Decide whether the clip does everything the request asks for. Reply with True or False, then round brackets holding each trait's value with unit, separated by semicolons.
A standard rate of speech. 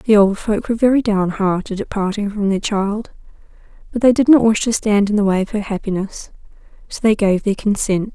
False (220 wpm)